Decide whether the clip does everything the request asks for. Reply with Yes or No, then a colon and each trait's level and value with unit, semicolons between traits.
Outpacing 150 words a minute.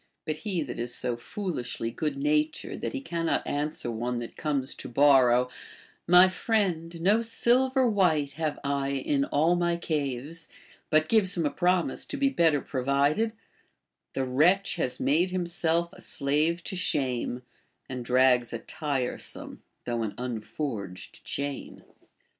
Yes: average, 160 wpm